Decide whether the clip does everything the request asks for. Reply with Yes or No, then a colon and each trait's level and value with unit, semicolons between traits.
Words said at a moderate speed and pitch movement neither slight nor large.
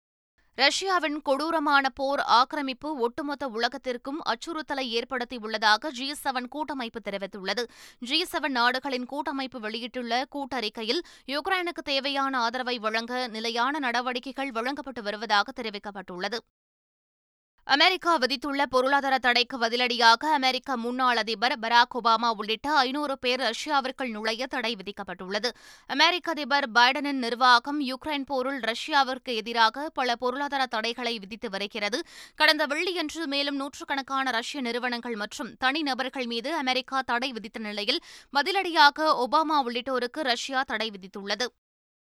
Yes: average, 105 wpm; average, 3.4 semitones